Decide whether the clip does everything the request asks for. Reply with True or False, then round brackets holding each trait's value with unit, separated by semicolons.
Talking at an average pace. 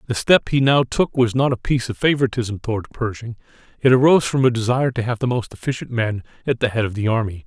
False (235 wpm)